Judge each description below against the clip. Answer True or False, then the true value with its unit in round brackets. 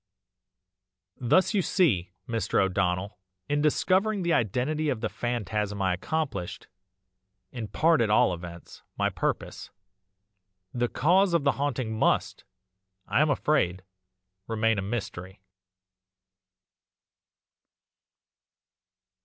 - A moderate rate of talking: False (105 wpm)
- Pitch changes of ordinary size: False (7.8 semitones)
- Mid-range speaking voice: False (120 Hz)